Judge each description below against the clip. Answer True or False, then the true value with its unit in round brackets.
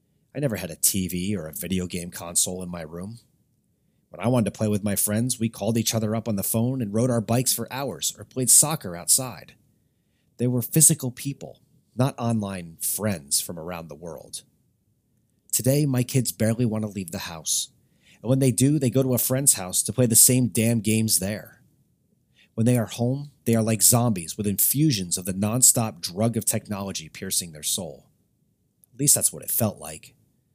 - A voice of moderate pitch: False (115 Hz)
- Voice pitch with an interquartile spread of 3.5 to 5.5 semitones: True (4.0 semitones)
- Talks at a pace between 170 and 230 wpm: True (200 wpm)